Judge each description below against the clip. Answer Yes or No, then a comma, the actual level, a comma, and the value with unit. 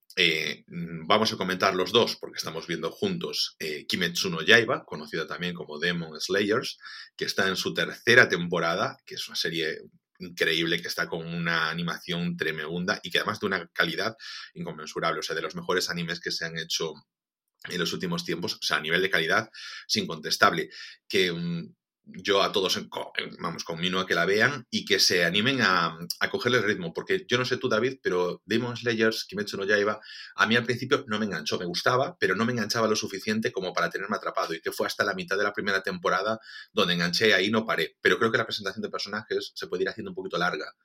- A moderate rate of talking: No, fast, 215 wpm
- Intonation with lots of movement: Yes, wide, 6.0 semitones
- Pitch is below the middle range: Yes, low, 100 Hz